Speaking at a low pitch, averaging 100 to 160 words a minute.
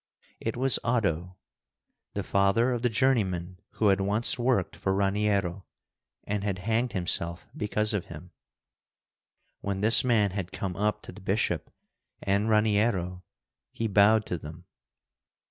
Yes: low, 100 Hz; average, 140 wpm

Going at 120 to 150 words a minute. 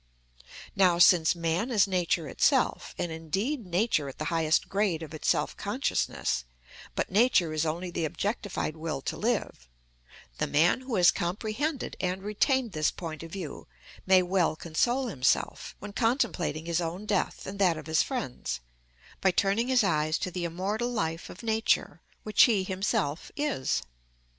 No: average, 160 wpm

